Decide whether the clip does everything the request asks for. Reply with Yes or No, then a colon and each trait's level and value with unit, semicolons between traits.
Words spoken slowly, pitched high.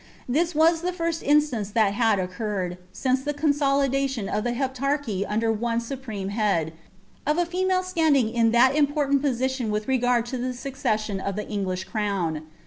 No: average, 165 wpm; high, 245 Hz